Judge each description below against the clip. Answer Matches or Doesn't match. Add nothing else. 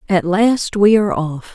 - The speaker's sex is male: Doesn't match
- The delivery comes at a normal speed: Matches